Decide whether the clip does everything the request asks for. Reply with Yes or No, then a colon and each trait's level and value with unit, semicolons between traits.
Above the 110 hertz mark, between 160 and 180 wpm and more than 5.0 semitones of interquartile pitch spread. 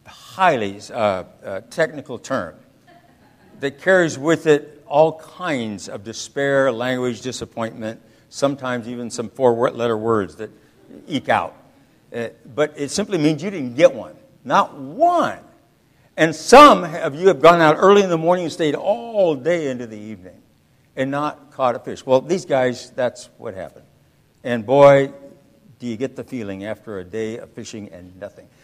Yes: medium, 140 Hz; average, 165 wpm; wide, 5.6 semitones